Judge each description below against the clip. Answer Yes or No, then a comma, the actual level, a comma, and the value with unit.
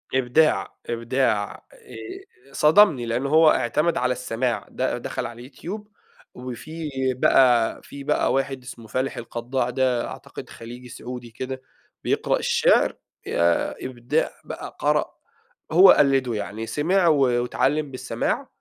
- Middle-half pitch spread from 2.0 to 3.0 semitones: No, average, 3.7 semitones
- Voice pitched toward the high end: No, low, 130 Hz